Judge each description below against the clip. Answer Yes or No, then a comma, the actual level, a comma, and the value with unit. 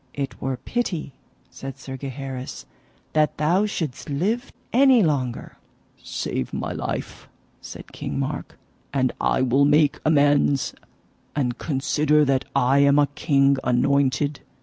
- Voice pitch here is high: No, medium, 140 Hz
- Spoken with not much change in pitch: Yes, narrow, 2.3 semitones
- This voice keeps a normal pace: No, slow, 125 wpm